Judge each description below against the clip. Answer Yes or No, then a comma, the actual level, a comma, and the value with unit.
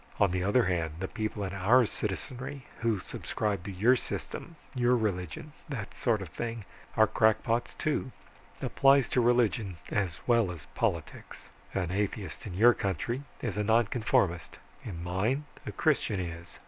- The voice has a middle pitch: No, low, 105 Hz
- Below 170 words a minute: Yes, average, 155 wpm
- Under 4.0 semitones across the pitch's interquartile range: No, average, 4.6 semitones